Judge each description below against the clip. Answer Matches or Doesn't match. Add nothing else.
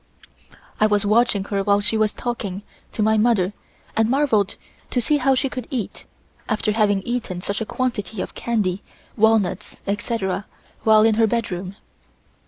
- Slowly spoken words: Doesn't match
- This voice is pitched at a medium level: Doesn't match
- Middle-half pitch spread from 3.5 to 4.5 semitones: Doesn't match